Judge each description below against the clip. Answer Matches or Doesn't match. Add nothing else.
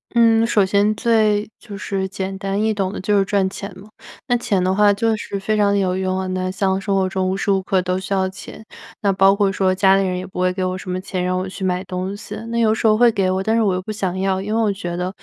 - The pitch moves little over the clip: Matches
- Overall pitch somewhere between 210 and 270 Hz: Doesn't match